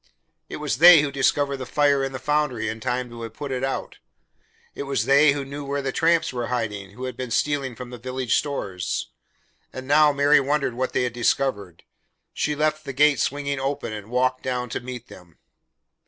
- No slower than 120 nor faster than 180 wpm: No, fast, 205 wpm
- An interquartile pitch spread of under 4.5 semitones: Yes, average, 2.7 semitones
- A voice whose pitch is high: No, low, 135 Hz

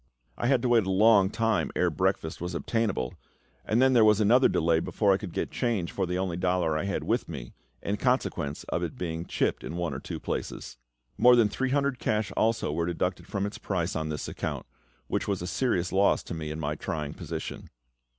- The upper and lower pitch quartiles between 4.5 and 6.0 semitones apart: Yes, average, 5.2 semitones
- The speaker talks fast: Yes, fast, 220 wpm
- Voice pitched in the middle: No, very low, 95 Hz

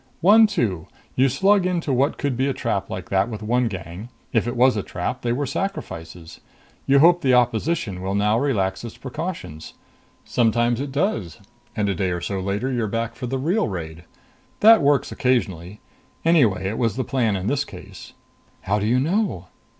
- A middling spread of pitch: No, wide, 6.2 semitones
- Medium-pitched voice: No, low, 120 Hz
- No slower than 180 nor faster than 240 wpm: Yes, average, 190 wpm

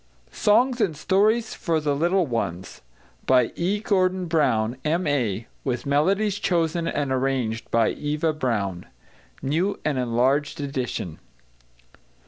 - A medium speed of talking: No, slow, 115 wpm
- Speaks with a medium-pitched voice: Yes, medium, 145 Hz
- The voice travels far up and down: Yes, wide, 6.2 semitones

